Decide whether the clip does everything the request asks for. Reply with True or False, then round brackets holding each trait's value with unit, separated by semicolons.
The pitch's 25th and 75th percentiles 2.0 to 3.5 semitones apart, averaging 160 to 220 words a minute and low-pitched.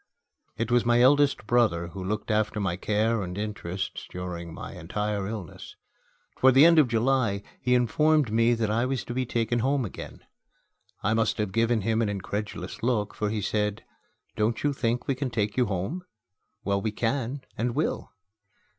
True (3.1 semitones; 180 wpm; 110 Hz)